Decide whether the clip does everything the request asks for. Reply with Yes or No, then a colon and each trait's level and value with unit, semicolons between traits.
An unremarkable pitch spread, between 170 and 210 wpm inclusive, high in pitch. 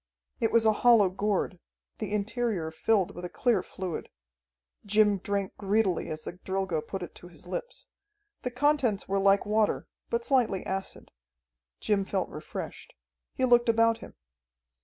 No: average, 3.3 semitones; average, 155 wpm; high, 200 Hz